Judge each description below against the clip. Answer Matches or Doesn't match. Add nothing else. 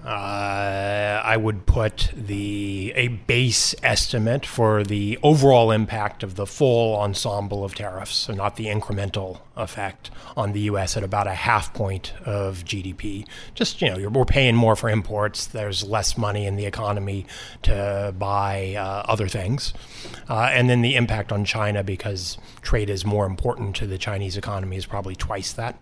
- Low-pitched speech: Matches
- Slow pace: Doesn't match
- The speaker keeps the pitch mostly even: Matches